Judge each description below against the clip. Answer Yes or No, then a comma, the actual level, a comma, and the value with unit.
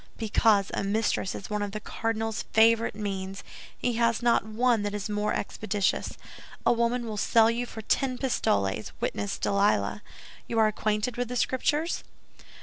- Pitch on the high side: Yes, high, 220 Hz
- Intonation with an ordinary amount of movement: No, narrow, 2.3 semitones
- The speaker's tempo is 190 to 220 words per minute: No, average, 160 wpm